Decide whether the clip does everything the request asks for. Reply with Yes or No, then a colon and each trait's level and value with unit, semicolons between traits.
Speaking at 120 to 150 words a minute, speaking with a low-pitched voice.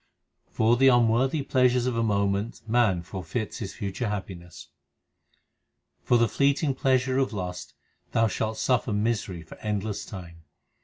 Yes: average, 140 wpm; low, 110 Hz